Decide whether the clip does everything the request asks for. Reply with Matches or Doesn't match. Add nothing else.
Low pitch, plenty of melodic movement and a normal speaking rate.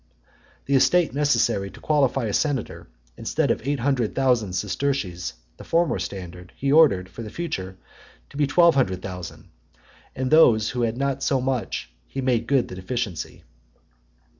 Matches